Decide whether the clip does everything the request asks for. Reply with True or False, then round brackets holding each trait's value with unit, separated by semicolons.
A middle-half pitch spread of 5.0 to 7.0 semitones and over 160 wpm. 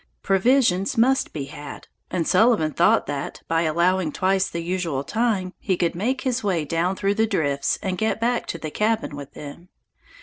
True (5.3 semitones; 180 wpm)